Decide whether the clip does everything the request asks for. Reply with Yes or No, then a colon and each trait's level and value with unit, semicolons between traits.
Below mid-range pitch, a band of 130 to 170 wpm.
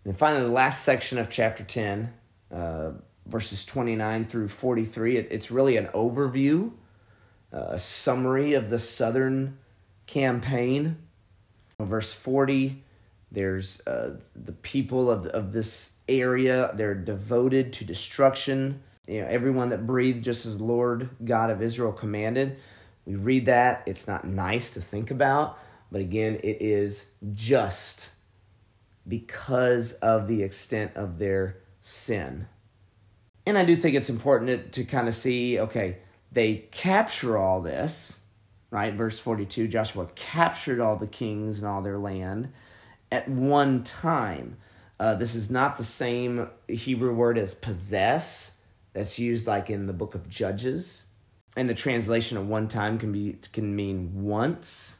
Yes: low, 110 Hz; average, 145 wpm